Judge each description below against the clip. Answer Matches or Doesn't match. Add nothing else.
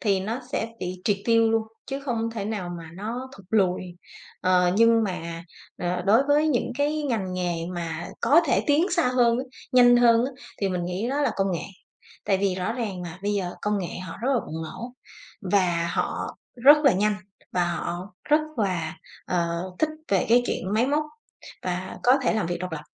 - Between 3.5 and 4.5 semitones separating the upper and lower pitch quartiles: Doesn't match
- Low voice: Doesn't match